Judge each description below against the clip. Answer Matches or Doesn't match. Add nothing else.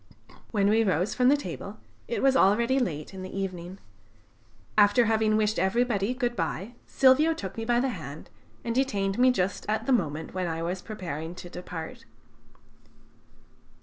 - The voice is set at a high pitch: Matches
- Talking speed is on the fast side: Doesn't match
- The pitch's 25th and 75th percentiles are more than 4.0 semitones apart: Matches